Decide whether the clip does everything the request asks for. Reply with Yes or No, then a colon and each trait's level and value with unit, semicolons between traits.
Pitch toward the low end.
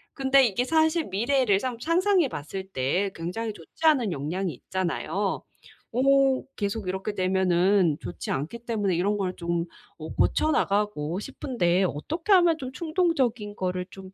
No: high, 205 Hz